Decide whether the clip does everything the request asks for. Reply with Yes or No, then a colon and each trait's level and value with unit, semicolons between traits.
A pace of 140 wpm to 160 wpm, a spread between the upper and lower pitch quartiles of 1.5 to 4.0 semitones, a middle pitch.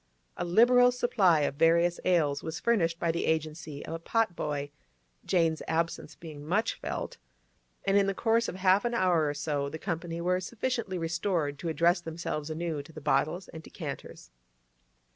No: average, 175 wpm; average, 3.1 semitones; medium, 170 Hz